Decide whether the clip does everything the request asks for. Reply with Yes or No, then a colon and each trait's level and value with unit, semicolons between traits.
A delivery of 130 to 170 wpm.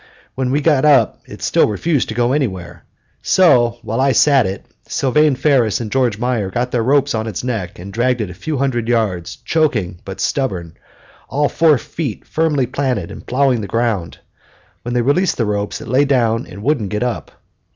No: average, 195 wpm